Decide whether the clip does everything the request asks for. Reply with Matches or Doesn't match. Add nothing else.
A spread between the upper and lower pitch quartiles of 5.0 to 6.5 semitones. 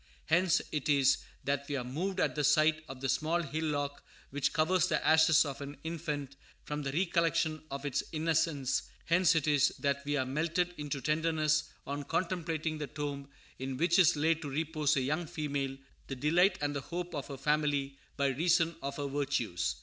Doesn't match